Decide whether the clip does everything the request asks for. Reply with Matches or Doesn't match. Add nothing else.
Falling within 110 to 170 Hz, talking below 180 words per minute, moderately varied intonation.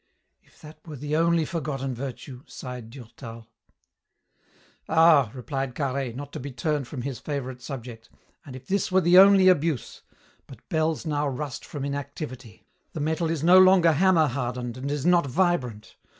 Matches